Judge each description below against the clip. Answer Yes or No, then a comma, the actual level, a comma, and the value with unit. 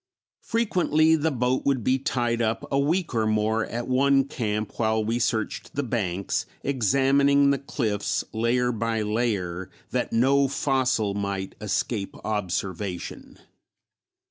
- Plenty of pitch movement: No, average, 4.4 semitones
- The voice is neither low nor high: No, low, 120 Hz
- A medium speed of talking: No, slow, 130 wpm